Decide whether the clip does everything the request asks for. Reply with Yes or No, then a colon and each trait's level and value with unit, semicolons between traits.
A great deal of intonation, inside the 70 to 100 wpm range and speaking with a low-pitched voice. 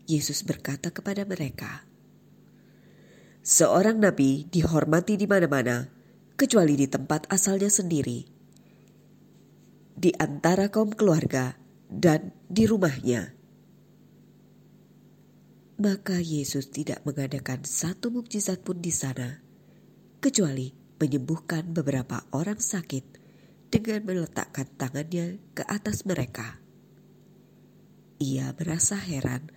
No: wide, 6.0 semitones; average, 90 wpm; medium, 160 Hz